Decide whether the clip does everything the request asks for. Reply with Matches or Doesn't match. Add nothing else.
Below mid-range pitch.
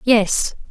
Doesn't match